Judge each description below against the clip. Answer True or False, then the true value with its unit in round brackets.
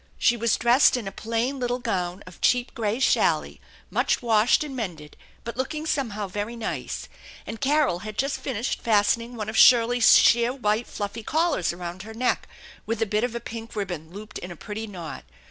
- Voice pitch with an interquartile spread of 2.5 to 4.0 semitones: True (3.2 semitones)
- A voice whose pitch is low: False (225 Hz)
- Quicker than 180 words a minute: True (190 wpm)